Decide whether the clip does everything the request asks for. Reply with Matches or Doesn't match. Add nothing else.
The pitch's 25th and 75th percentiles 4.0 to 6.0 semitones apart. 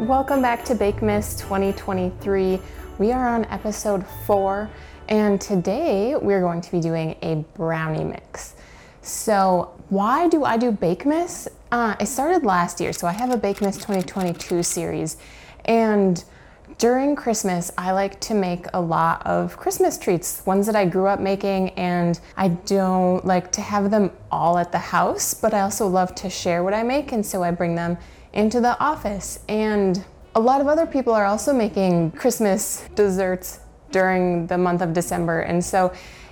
Doesn't match